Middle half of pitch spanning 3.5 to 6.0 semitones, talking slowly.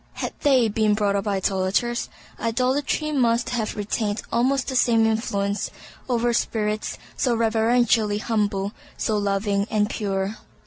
No: average, 2.7 semitones; slow, 130 wpm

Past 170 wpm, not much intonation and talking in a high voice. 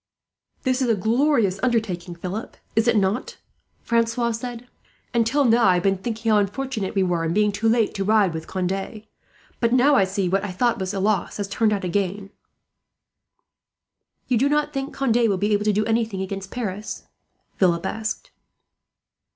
No: average, 185 wpm; average, 3.4 semitones; high, 215 Hz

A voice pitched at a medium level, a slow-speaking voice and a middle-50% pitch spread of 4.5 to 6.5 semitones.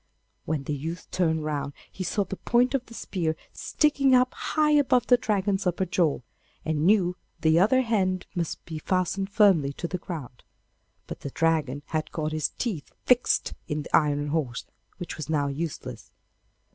No: medium, 170 Hz; average, 175 wpm; average, 5.0 semitones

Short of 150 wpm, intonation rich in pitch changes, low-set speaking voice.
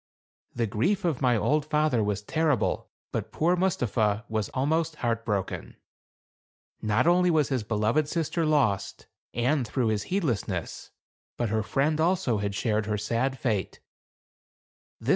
Yes: average, 140 wpm; wide, 6.3 semitones; low, 125 Hz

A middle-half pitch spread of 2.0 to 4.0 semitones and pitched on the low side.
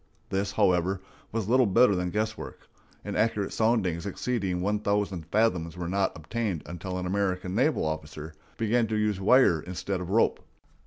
Yes: average, 3.4 semitones; low, 100 Hz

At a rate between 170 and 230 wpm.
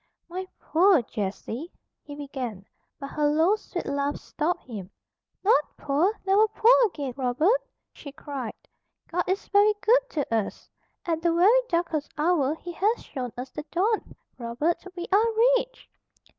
No: average, 150 wpm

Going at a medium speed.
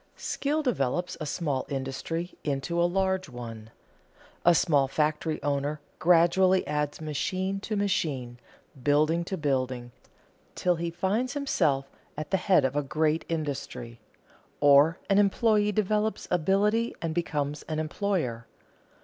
No: slow, 130 wpm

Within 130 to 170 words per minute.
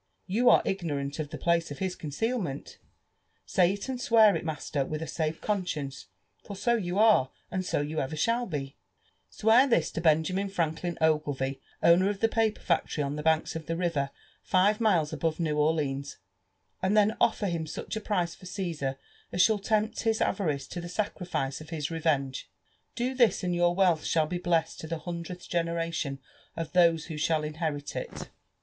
No: average, 185 wpm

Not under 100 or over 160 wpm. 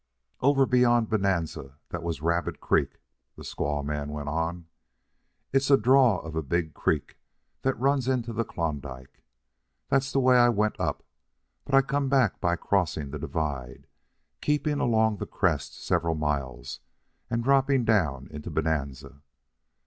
Yes: average, 150 wpm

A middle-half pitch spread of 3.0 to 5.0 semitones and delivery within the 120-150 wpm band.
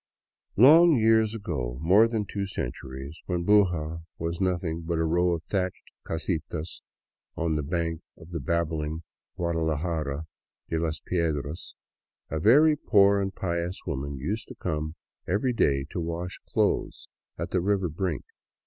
Yes: average, 3.7 semitones; average, 145 wpm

